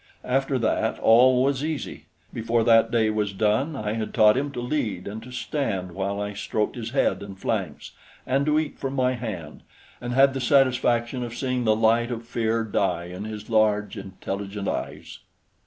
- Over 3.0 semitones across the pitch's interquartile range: Yes, average, 3.4 semitones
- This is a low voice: Yes, low, 115 Hz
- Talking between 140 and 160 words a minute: No, average, 185 wpm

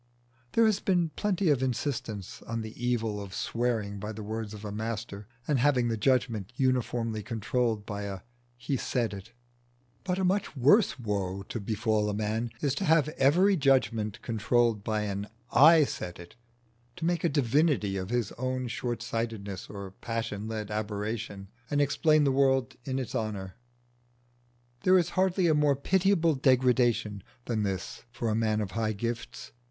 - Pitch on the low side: Yes, low, 115 Hz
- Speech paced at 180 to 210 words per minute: No, average, 170 wpm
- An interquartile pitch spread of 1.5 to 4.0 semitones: No, average, 4.7 semitones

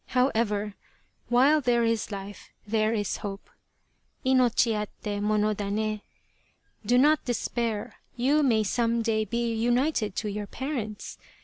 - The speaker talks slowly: Yes, slow, 130 wpm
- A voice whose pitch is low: No, high, 225 Hz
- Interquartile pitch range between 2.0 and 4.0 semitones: Yes, narrow, 2.6 semitones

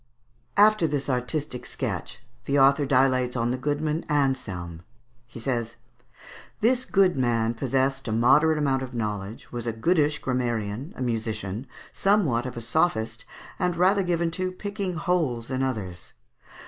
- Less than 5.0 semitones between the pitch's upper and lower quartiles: No, average, 5.3 semitones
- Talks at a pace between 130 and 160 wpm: Yes, average, 145 wpm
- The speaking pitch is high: No, low, 130 Hz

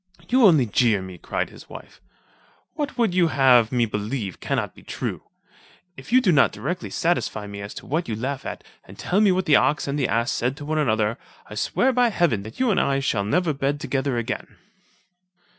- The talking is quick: Yes, fast, 210 wpm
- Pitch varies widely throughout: Yes, wide, 7.6 semitones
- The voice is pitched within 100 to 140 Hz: Yes, low, 135 Hz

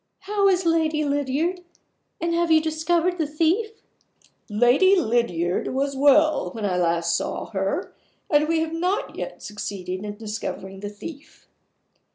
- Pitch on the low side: No, very high, 295 Hz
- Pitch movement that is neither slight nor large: No, wide, 8.2 semitones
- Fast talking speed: No, average, 145 wpm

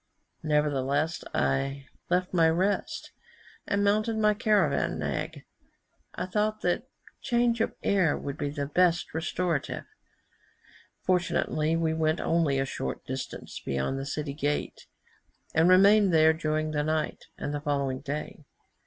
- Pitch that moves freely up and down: No, average, 4.1 semitones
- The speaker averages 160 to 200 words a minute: No, slow, 135 wpm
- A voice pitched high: No, medium, 160 Hz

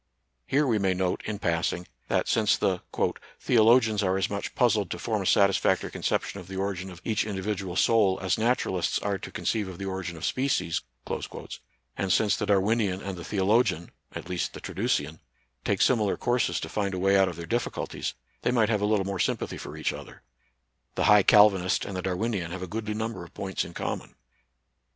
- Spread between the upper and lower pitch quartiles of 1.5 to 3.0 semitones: Yes, average, 2.7 semitones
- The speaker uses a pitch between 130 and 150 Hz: No, low, 100 Hz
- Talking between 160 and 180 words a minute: No, fast, 205 wpm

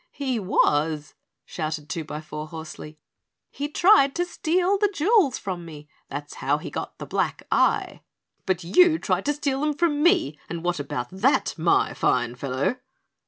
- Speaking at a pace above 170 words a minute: No, average, 160 wpm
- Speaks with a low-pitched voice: No, medium, 185 Hz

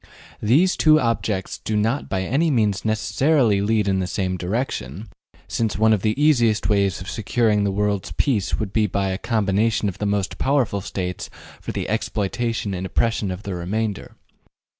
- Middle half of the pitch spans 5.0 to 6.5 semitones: No, average, 2.9 semitones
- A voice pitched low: Yes, low, 105 Hz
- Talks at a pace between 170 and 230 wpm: Yes, average, 175 wpm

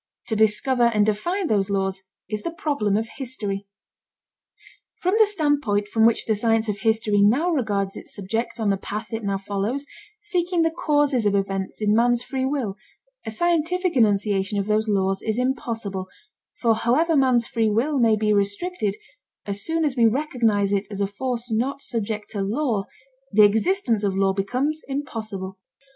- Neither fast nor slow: Yes, average, 170 wpm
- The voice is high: Yes, high, 220 Hz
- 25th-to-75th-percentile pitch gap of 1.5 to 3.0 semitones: No, average, 4.8 semitones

